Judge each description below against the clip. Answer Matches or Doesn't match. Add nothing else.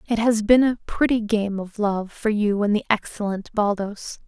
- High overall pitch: Matches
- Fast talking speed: Doesn't match